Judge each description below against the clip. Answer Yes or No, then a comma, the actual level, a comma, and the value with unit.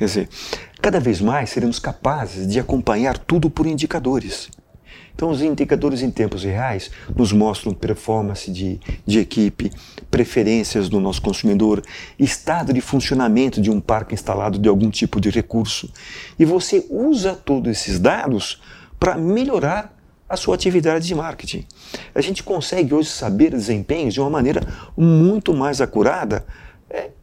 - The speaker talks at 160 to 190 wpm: No, average, 145 wpm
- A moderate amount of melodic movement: No, wide, 7.2 semitones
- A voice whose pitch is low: Yes, low, 130 Hz